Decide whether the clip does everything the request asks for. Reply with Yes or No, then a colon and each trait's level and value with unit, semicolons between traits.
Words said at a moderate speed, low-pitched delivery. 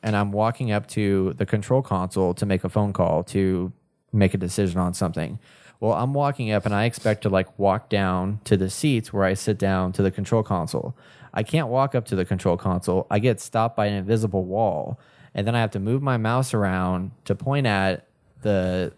No: fast, 220 wpm; low, 100 Hz